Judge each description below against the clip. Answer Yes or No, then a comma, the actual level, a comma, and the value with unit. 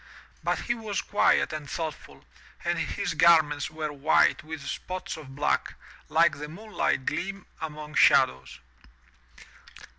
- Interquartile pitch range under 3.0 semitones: Yes, narrow, 2.6 semitones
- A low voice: No, medium, 155 Hz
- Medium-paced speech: No, slow, 125 wpm